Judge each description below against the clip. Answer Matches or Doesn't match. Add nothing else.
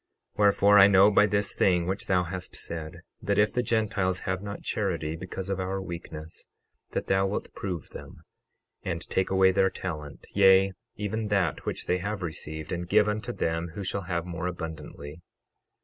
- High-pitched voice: Doesn't match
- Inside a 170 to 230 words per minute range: Matches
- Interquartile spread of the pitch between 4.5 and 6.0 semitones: Doesn't match